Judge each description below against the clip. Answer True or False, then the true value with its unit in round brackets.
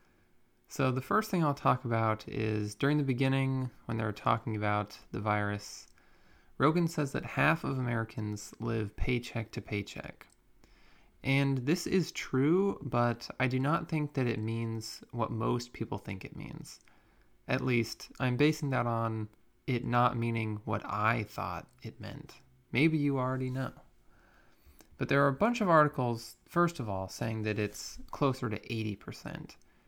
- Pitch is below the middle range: True (120 Hz)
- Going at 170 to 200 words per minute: False (160 wpm)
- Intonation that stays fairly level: False (3.9 semitones)